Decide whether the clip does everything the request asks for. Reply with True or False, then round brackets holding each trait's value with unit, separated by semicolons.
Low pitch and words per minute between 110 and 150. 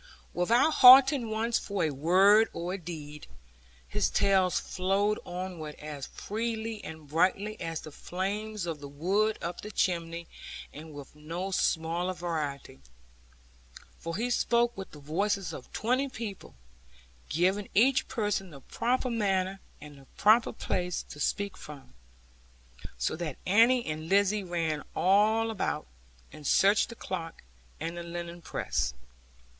False (185 Hz; 140 wpm)